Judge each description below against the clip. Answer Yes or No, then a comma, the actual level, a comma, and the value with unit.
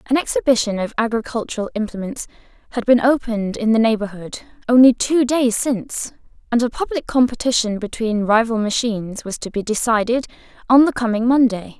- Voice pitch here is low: No, high, 230 Hz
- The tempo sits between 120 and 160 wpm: Yes, average, 155 wpm